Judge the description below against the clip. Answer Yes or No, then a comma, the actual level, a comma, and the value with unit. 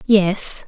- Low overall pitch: No, high, 195 Hz